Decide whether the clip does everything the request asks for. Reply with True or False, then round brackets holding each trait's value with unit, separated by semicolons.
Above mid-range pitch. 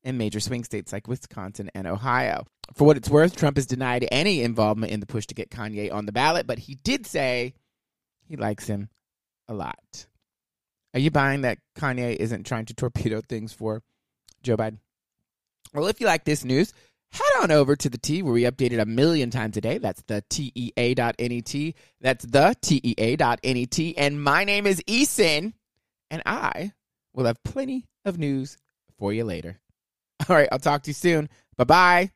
False (125 Hz)